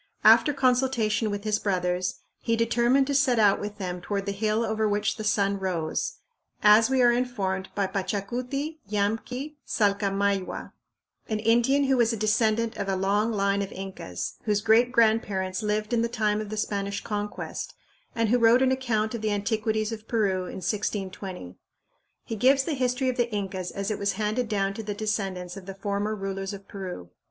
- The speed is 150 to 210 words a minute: Yes, average, 185 wpm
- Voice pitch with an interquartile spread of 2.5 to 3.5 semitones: Yes, average, 2.9 semitones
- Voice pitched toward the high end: Yes, high, 210 Hz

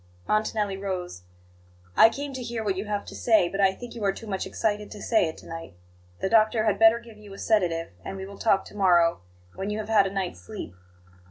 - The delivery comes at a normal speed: No, fast, 240 wpm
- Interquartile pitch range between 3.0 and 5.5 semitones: No, narrow, 2.5 semitones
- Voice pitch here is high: Yes, high, 205 Hz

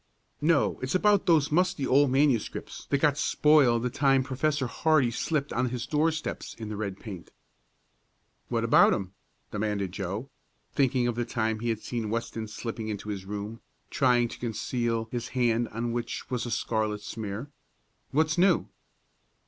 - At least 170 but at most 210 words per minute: No, average, 160 wpm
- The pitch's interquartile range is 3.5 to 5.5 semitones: Yes, average, 4.3 semitones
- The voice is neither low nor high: No, low, 120 Hz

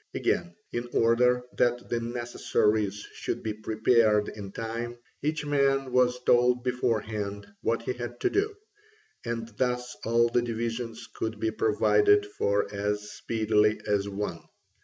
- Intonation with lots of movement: No, narrow, 2.5 semitones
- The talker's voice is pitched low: Yes, low, 115 Hz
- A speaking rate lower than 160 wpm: Yes, average, 140 wpm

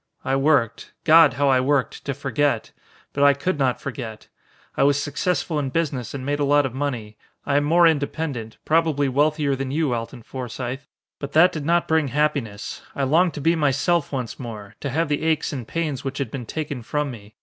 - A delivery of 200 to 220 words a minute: Yes, fast, 205 wpm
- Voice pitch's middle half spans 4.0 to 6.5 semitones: No, average, 2.9 semitones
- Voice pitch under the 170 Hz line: Yes, medium, 140 Hz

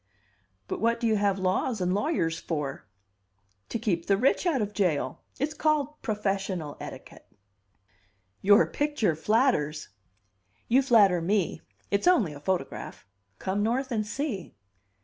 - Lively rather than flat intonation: Yes, wide, 5.8 semitones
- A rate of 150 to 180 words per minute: No, slow, 135 wpm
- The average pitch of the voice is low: No, high, 205 Hz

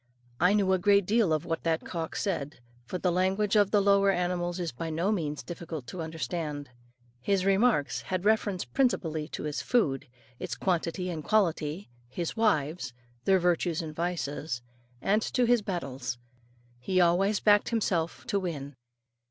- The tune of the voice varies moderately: Yes, average, 4.0 semitones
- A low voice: No, medium, 175 Hz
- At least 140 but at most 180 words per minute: Yes, average, 160 wpm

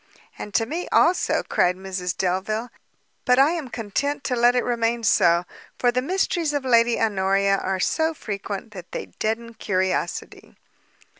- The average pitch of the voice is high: Yes, high, 230 Hz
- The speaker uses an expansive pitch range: No, average, 4.7 semitones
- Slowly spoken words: No, average, 155 wpm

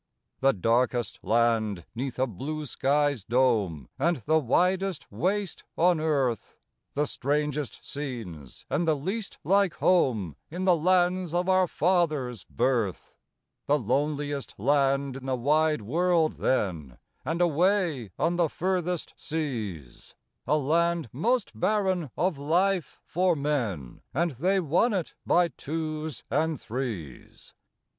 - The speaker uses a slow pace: Yes, slow, 125 wpm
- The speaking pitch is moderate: Yes, medium, 150 Hz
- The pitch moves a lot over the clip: Yes, wide, 5.9 semitones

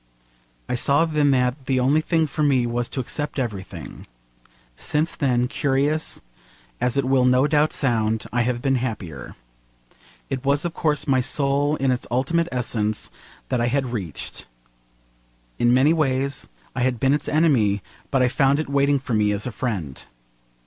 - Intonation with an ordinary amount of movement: Yes, average, 3.0 semitones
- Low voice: Yes, low, 130 Hz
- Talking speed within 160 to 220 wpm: Yes, average, 170 wpm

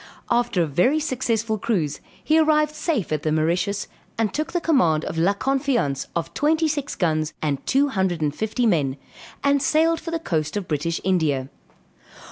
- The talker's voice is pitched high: Yes, high, 210 Hz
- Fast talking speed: No, average, 175 wpm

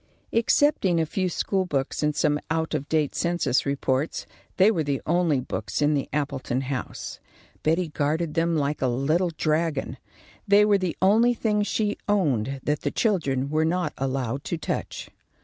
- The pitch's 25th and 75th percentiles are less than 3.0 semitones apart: No, average, 4.6 semitones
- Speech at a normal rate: Yes, average, 165 wpm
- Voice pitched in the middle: Yes, medium, 155 Hz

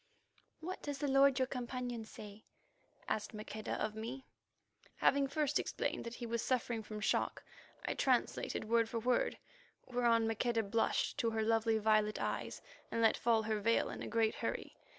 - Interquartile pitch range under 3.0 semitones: Yes, narrow, 2.4 semitones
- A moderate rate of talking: Yes, average, 170 wpm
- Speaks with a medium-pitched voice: No, high, 230 Hz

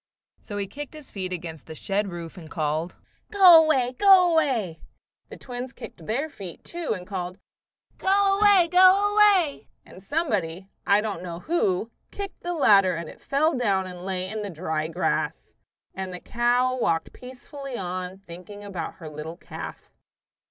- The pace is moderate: Yes, average, 165 wpm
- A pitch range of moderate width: No, wide, 9.0 semitones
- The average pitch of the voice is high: Yes, high, 205 Hz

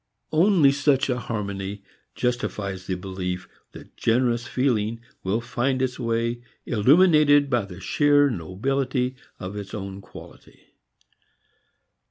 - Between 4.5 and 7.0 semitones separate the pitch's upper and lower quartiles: Yes, wide, 5.5 semitones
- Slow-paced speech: Yes, slow, 115 wpm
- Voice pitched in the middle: No, low, 120 Hz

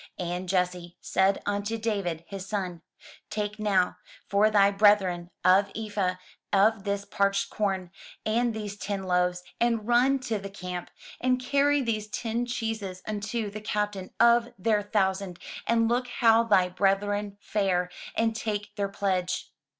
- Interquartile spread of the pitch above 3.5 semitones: No, average, 2.7 semitones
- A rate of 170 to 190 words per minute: No, average, 145 wpm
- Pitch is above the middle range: Yes, high, 205 Hz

